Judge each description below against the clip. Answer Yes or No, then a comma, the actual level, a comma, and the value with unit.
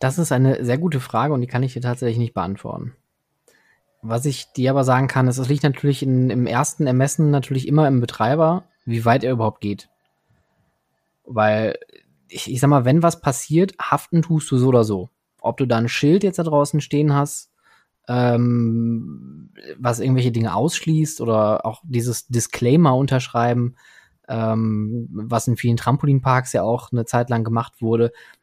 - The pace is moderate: Yes, average, 175 wpm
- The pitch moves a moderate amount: Yes, average, 3.4 semitones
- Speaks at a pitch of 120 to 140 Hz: Yes, low, 125 Hz